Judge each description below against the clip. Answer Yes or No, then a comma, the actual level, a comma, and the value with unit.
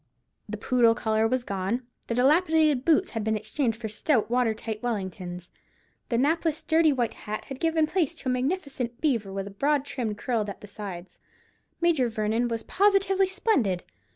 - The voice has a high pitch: Yes, high, 245 Hz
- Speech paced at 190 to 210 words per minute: No, average, 175 wpm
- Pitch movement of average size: No, wide, 6.1 semitones